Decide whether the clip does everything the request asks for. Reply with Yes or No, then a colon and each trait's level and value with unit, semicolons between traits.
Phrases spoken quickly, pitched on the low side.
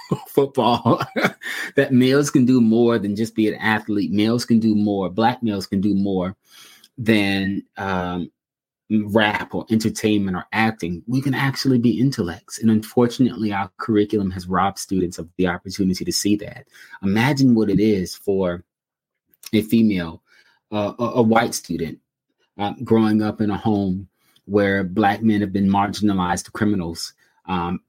No: average, 155 wpm; low, 105 Hz